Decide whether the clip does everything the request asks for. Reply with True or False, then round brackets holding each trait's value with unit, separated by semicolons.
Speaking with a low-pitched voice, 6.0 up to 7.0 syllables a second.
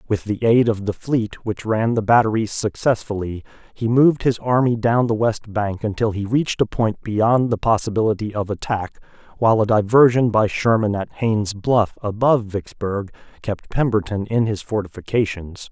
False (110 Hz; 5.0 syllables/s)